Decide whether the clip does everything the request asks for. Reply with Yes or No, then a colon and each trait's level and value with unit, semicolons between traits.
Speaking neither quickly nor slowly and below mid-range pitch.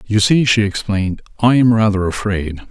Yes: average, 175 wpm; low, 105 Hz